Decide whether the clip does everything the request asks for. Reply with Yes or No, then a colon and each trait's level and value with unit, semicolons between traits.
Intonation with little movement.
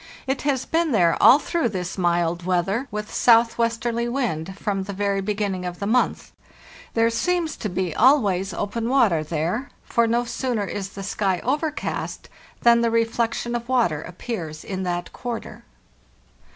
No: average, 4.4 semitones